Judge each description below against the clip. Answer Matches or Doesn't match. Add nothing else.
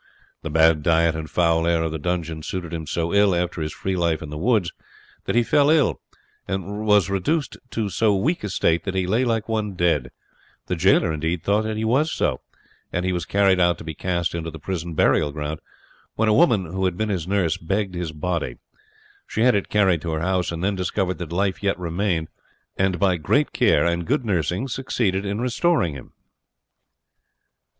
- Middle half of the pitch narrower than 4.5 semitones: Matches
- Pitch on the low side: Matches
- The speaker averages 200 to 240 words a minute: Matches